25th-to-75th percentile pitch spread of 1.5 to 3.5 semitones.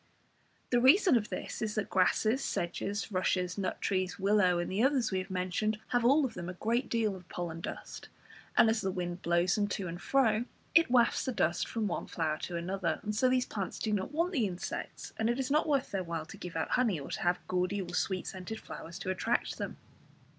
No: average, 4.6 semitones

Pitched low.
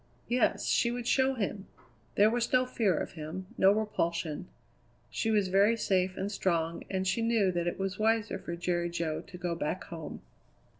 No: high, 190 Hz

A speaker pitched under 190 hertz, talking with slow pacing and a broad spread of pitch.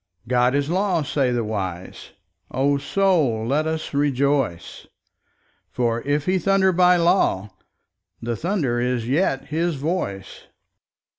Yes: medium, 140 Hz; slow, 125 wpm; wide, 6.2 semitones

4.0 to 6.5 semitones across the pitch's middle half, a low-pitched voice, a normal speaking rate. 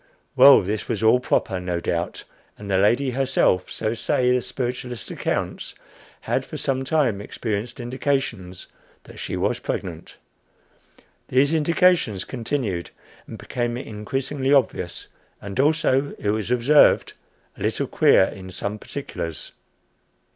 No: average, 4.9 semitones; low, 120 Hz; slow, 130 wpm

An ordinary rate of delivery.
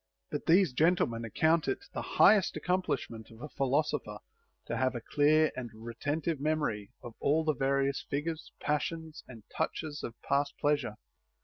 Yes: average, 155 wpm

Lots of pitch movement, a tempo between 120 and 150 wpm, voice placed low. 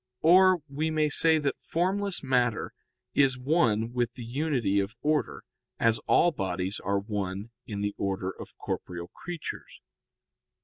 Yes: wide, 7.4 semitones; average, 140 wpm; low, 125 Hz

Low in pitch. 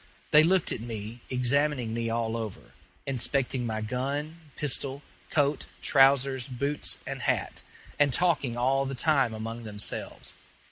Yes: low, 130 Hz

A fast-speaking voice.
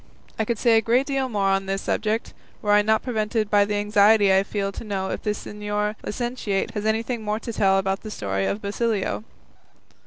Yes: fast, 210 wpm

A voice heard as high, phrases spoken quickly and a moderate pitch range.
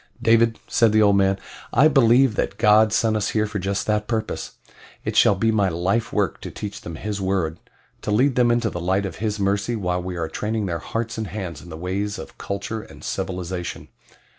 No: low, 105 Hz; fast, 215 wpm; average, 3.0 semitones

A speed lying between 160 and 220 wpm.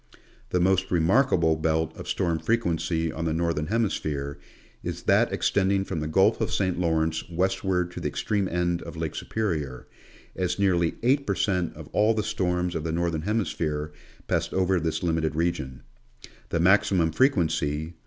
Yes: average, 175 wpm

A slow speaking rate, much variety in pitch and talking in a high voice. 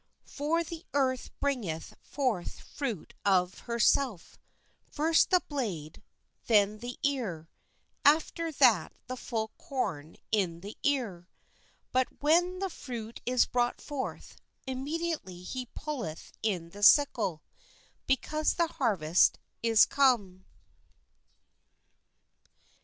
Yes: slow, 110 wpm; wide, 6.8 semitones; high, 245 Hz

